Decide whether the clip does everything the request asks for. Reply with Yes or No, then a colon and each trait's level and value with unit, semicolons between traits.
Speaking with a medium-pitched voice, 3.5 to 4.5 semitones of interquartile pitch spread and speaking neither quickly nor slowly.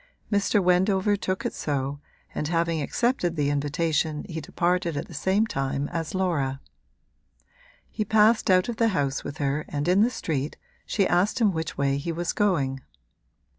No: medium, 170 Hz; average, 4.9 semitones; average, 170 wpm